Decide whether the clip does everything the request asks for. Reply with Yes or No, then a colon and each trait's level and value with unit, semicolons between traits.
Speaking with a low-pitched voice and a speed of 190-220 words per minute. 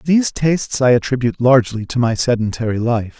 No: low, 125 Hz; average, 170 wpm